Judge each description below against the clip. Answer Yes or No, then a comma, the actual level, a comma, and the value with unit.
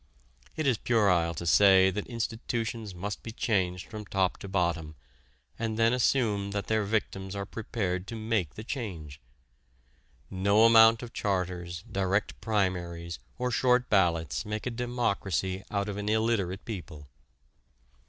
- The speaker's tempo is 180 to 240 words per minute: No, average, 145 wpm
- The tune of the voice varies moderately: Yes, average, 3.6 semitones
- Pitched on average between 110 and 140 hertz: No, low, 100 Hz